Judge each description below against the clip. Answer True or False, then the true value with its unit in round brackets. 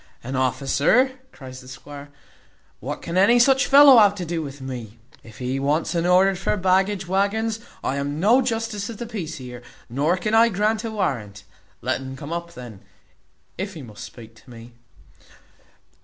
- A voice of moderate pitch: True (170 Hz)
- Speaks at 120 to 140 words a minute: False (175 wpm)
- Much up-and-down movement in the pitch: True (8.0 semitones)